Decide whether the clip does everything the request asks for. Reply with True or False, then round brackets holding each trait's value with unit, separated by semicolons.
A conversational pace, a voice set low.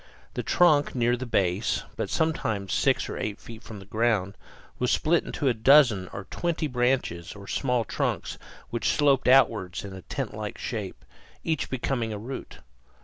True (165 wpm; 120 Hz)